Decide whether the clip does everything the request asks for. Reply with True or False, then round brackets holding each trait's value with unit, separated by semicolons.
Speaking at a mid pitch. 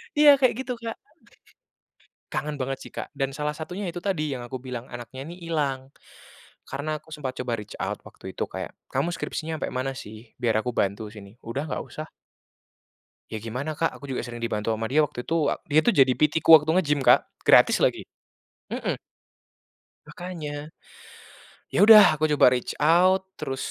True (145 Hz)